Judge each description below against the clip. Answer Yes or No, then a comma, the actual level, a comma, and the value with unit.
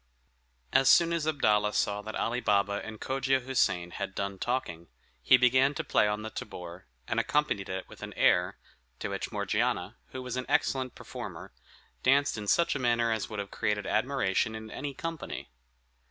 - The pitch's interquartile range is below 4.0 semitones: No, average, 4.6 semitones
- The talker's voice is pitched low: Yes, low, 115 Hz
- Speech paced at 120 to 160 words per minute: No, average, 180 wpm